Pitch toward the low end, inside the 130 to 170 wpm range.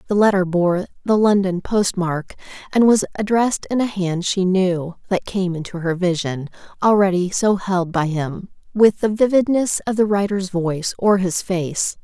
No: high, 190 Hz; average, 165 wpm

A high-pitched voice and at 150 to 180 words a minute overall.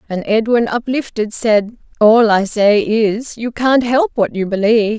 Yes: high, 220 Hz; average, 155 wpm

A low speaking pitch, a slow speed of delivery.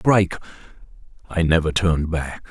Yes: very low, 85 Hz; slow, 120 wpm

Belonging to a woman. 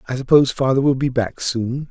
No: male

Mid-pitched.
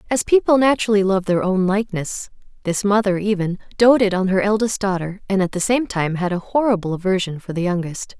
No: high, 200 Hz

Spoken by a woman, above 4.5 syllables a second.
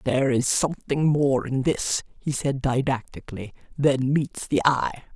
No: female; 4.4 syllables/s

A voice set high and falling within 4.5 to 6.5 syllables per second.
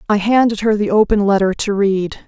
Yes: high, 205 Hz; 5.4 syllables/s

